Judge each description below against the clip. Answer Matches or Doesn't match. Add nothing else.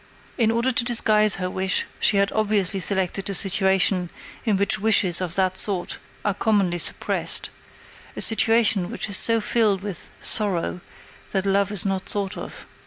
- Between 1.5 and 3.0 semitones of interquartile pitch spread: Matches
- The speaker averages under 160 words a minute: Doesn't match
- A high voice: Matches